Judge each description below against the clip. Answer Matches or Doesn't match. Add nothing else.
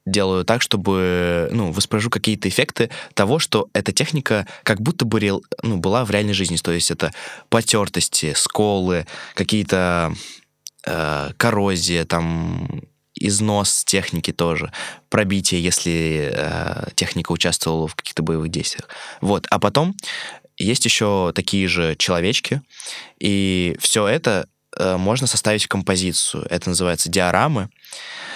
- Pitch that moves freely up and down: Doesn't match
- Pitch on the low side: Matches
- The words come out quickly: Doesn't match